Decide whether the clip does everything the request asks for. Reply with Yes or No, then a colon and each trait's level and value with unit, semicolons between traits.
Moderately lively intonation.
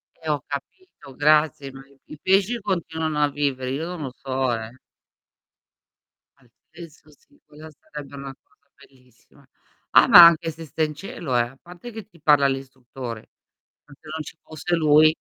Yes: average, 3.2 semitones